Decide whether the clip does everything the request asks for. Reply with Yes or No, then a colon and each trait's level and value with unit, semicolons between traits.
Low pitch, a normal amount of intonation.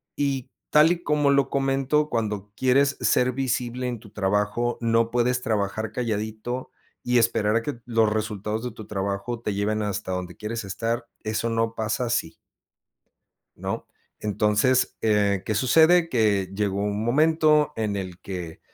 Yes: low, 115 Hz; average, 3.4 semitones